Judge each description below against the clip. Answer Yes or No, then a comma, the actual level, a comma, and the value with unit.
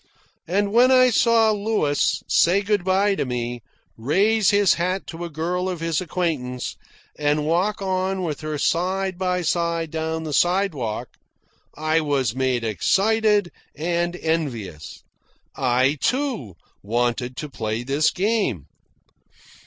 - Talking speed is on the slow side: Yes, slow, 130 wpm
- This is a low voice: No, medium, 165 Hz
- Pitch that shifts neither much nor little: No, wide, 6.3 semitones